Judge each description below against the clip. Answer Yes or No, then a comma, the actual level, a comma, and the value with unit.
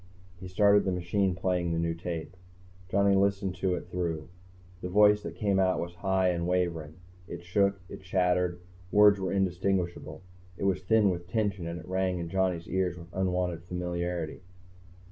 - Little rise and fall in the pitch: Yes, narrow, 1.8 semitones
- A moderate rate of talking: Yes, average, 170 wpm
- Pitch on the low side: Yes, very low, 90 Hz